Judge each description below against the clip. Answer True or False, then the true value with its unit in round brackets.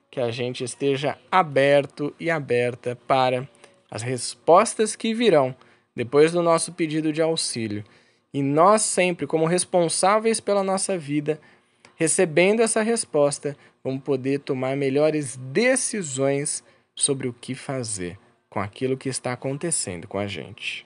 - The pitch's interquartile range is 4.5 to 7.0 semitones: True (5.2 semitones)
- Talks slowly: False (130 wpm)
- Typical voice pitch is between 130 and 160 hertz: True (140 Hz)